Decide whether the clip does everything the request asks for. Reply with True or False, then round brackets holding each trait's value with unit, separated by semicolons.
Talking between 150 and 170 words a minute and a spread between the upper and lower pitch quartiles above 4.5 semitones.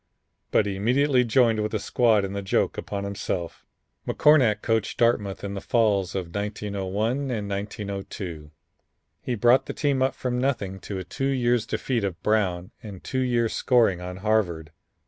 False (165 wpm; 3.8 semitones)